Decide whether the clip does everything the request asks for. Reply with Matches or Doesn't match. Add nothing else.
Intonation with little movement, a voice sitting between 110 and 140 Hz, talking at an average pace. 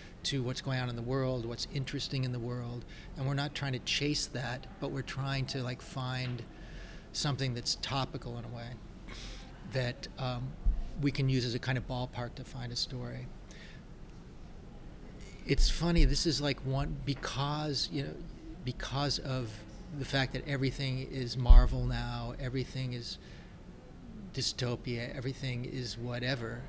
Matches